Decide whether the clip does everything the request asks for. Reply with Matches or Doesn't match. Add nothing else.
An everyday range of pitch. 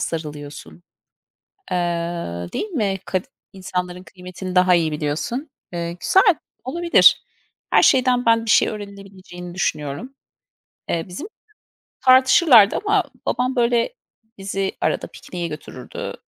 Doesn't match